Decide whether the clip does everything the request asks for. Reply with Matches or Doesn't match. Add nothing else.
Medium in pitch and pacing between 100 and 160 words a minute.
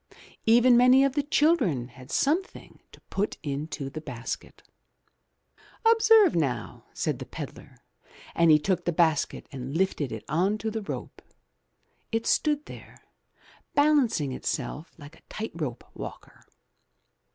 Matches